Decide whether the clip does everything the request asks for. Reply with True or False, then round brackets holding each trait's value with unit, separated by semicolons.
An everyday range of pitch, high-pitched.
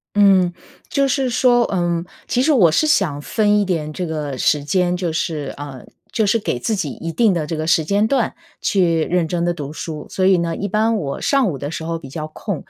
False (4.9 semitones; 175 Hz)